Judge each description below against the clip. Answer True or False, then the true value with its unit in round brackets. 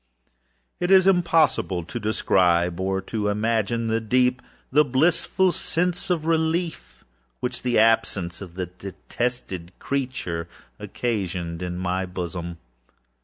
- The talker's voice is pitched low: True (110 Hz)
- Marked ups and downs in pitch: True (7.5 semitones)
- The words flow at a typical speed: False (120 wpm)